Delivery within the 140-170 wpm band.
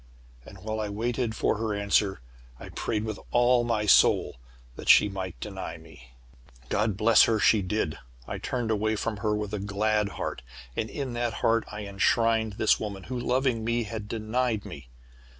No: average, 180 wpm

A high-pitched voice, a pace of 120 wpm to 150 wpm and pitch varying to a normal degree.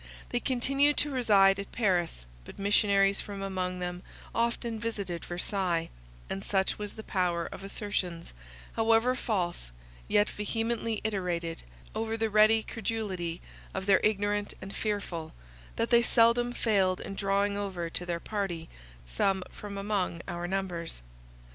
Yes: high, 200 Hz; slow, 135 wpm; average, 3.7 semitones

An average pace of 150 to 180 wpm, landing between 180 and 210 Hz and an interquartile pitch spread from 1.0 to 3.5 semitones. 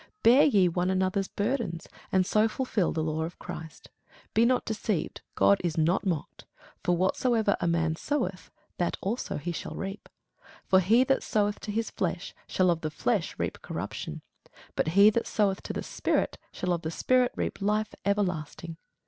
No: average, 175 wpm; high, 190 Hz; average, 4.2 semitones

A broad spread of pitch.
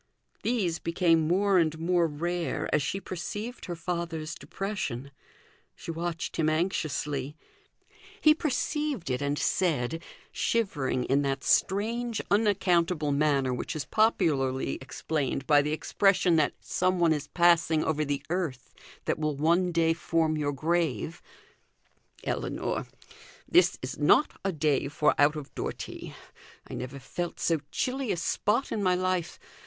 No: average, 4.0 semitones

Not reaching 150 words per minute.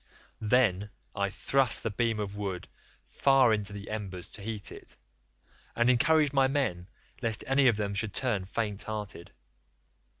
No: average, 155 wpm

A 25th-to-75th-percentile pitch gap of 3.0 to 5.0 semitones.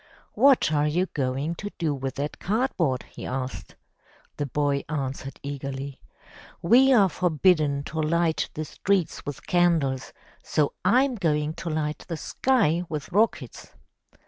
Yes: average, 4.2 semitones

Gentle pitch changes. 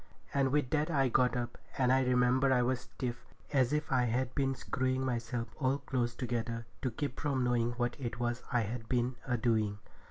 Yes: narrow, 1.6 semitones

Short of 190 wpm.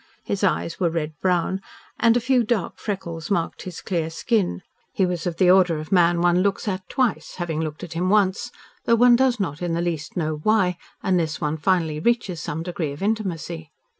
No: average, 200 wpm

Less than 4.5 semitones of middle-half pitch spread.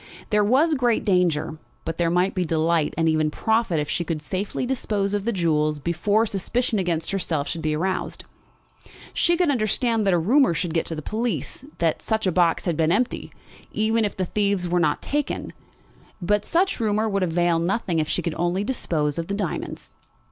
No: average, 4.8 semitones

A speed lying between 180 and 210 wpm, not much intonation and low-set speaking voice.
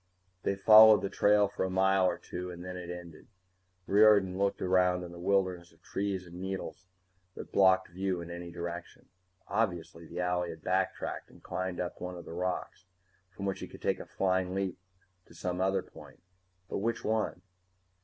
Yes: average, 185 wpm; narrow, 1.7 semitones; very low, 95 Hz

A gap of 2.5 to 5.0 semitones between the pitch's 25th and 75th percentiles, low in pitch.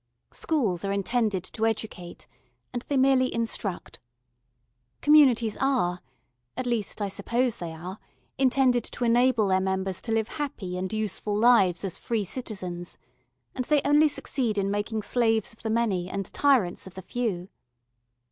No: average, 4.6 semitones; high, 220 Hz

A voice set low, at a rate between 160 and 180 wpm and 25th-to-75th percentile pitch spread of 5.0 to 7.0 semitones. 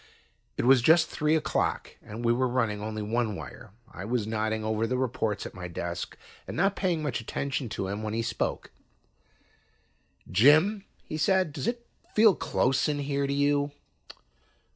Yes: low, 125 Hz; average, 170 wpm; wide, 5.6 semitones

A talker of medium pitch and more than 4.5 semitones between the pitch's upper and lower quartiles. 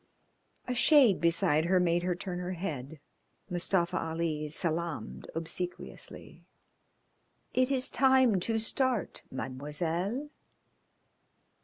Yes: medium, 175 Hz; wide, 5.4 semitones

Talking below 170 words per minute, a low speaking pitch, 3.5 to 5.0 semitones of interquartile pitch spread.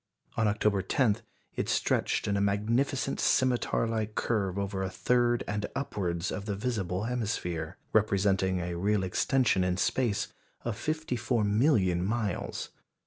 Yes: average, 140 wpm; low, 105 Hz; average, 3.9 semitones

